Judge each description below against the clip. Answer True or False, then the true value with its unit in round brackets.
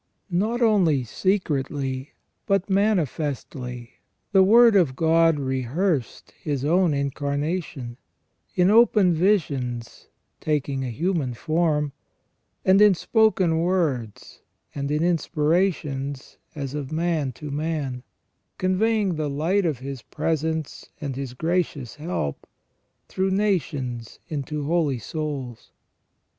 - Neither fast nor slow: False (110 wpm)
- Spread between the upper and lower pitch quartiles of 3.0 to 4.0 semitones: False (5.0 semitones)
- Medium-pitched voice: True (155 Hz)